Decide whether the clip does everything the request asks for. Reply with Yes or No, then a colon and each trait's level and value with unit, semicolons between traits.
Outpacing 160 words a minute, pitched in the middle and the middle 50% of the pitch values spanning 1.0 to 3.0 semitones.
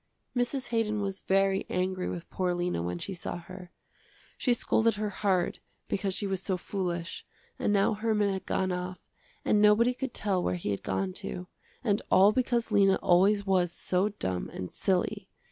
No: average, 180 wpm; high, 195 Hz; narrow, 2.6 semitones